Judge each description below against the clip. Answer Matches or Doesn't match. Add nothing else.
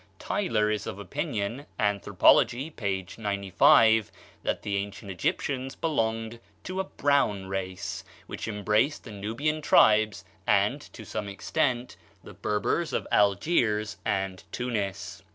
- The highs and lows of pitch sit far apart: Doesn't match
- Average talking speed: Doesn't match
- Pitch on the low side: Matches